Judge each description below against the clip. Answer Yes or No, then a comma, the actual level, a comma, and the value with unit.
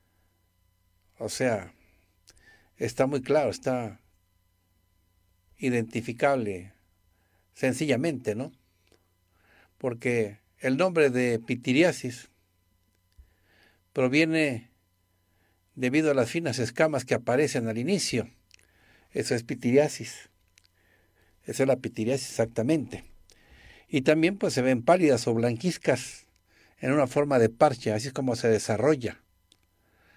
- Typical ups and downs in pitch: No, wide, 6.2 semitones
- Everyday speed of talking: No, slow, 100 wpm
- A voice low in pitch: Yes, low, 110 Hz